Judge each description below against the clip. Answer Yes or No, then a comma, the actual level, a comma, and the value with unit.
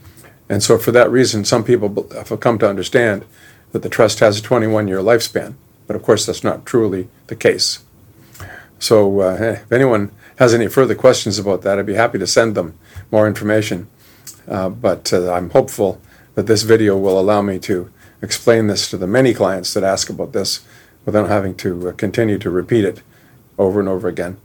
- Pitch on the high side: No, low, 105 Hz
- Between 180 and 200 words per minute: Yes, average, 190 wpm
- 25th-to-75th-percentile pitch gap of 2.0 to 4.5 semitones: Yes, average, 3.1 semitones